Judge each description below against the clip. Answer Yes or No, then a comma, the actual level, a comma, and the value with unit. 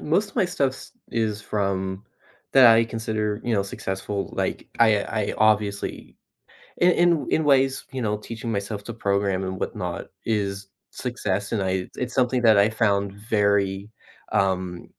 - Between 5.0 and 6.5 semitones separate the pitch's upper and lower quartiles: No, average, 3.1 semitones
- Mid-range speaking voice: No, low, 105 Hz